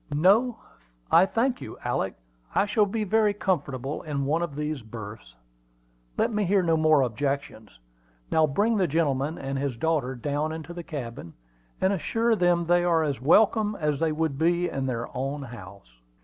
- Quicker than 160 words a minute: Yes, average, 175 wpm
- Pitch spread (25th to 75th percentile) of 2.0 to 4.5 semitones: No, average, 5.1 semitones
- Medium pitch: Yes, medium, 155 Hz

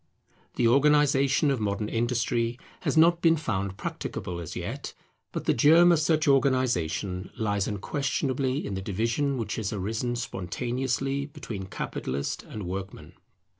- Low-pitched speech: Yes, low, 120 Hz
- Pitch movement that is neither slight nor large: No, wide, 5.8 semitones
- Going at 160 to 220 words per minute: No, slow, 135 wpm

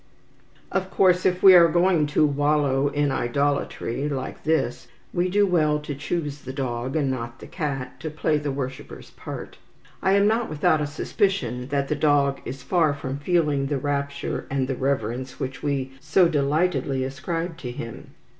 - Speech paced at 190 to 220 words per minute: No, average, 175 wpm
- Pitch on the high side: No, medium, 145 Hz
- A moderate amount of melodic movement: Yes, average, 3.4 semitones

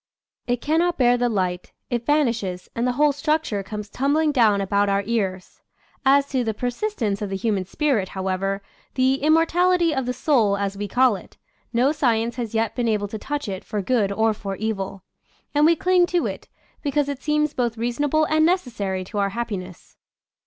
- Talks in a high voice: Yes, high, 235 Hz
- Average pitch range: No, wide, 6.4 semitones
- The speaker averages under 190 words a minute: No, average, 200 wpm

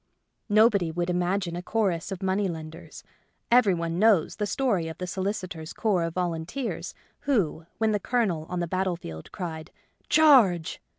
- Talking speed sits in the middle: Yes, average, 170 wpm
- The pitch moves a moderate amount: Yes, average, 3.8 semitones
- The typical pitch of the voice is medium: Yes, medium, 180 Hz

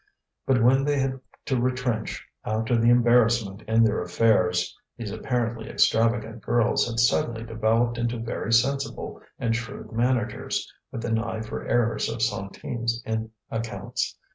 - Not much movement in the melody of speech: Yes, narrow, 1.4 semitones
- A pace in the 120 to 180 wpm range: Yes, average, 140 wpm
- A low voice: Yes, low, 115 Hz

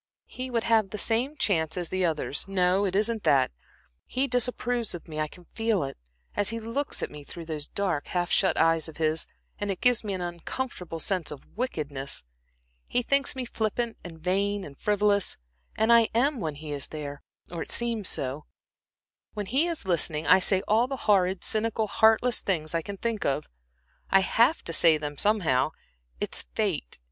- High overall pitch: Yes, high, 195 Hz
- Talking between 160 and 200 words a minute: Yes, average, 190 wpm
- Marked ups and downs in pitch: Yes, wide, 6.1 semitones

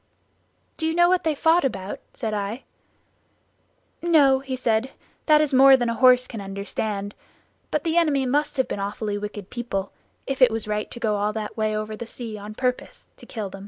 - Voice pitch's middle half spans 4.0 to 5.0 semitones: Yes, average, 4.4 semitones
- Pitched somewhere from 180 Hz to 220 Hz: No, high, 235 Hz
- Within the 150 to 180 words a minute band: No, average, 200 wpm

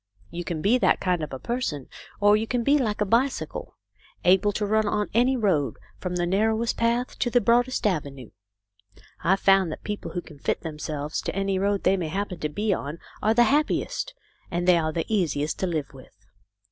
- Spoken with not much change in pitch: No, wide, 5.6 semitones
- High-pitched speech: Yes, high, 195 Hz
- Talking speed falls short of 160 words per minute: No, fast, 205 wpm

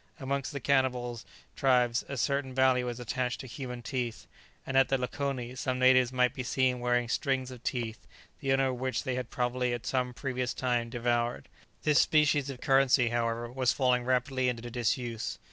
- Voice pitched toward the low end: Yes, low, 125 Hz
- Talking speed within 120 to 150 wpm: No, average, 180 wpm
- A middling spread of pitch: No, narrow, 1.5 semitones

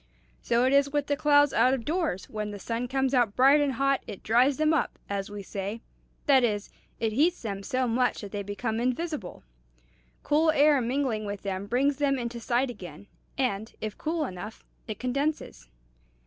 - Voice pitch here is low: No, very high, 250 Hz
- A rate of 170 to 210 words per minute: Yes, average, 190 wpm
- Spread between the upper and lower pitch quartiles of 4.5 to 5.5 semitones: Yes, average, 4.9 semitones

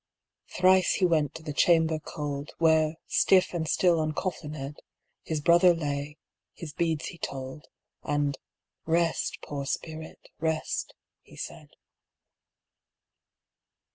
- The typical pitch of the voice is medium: Yes, medium, 160 Hz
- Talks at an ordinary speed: No, slow, 110 wpm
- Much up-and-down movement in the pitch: No, narrow, 2.4 semitones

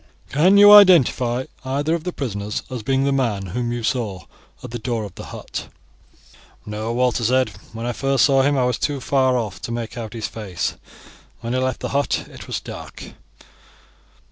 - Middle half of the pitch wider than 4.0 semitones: No, average, 3.2 semitones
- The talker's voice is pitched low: Yes, low, 125 Hz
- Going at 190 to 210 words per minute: Yes, average, 195 wpm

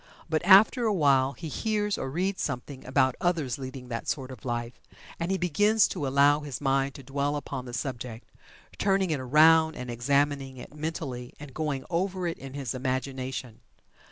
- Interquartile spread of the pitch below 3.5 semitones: No, average, 3.9 semitones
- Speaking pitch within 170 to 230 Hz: No, medium, 140 Hz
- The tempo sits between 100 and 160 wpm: No, average, 180 wpm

